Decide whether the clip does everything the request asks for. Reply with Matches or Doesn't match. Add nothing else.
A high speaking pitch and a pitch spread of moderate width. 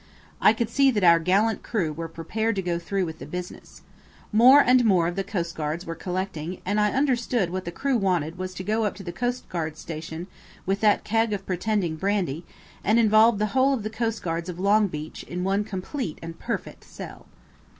Matches